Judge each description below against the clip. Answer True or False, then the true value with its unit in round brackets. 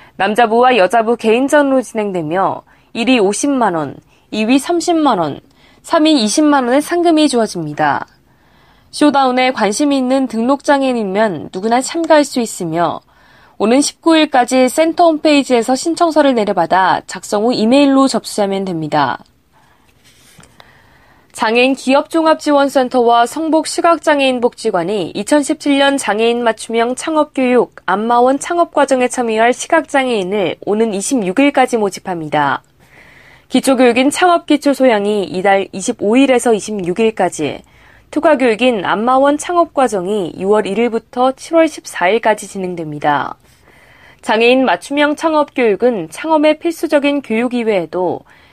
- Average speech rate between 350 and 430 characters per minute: False (280 characters per minute)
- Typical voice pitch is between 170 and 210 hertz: False (245 Hz)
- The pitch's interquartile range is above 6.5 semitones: False (5.7 semitones)